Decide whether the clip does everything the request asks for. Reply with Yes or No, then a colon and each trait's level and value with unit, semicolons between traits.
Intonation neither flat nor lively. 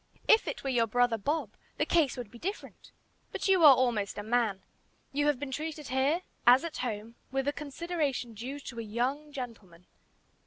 Yes: average, 4.2 semitones